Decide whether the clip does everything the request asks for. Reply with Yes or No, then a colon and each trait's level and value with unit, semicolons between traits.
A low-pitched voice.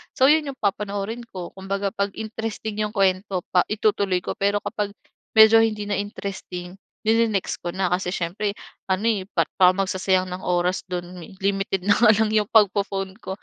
No: high, 200 Hz